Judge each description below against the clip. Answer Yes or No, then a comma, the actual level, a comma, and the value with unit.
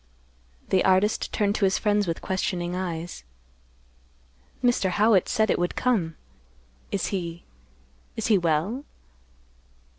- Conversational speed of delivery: No, slow, 115 wpm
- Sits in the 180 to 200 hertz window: Yes, medium, 185 Hz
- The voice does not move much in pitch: No, average, 3.7 semitones